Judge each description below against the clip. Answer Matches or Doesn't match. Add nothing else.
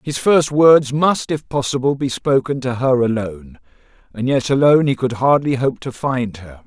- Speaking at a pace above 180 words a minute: Matches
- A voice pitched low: Matches